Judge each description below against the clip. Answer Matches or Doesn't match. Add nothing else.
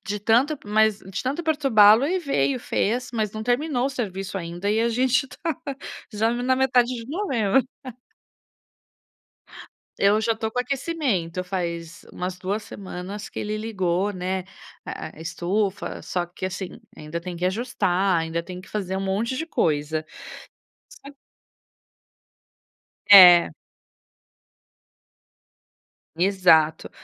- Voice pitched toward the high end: Matches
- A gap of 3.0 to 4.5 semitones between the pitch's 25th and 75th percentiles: Doesn't match